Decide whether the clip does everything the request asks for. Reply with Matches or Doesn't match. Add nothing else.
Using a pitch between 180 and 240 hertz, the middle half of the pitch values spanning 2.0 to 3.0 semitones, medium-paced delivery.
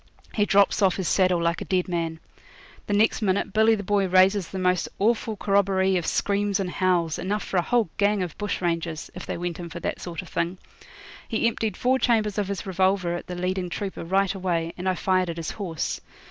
Doesn't match